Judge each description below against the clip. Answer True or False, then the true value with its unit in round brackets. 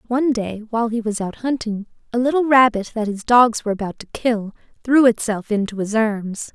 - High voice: True (225 Hz)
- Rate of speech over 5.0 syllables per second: True (5.5 syllables/s)